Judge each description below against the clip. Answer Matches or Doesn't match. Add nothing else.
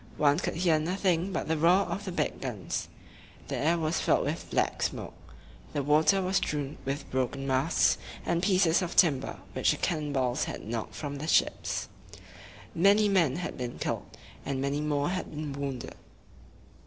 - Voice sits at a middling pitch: Matches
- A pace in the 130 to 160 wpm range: Doesn't match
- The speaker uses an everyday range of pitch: Matches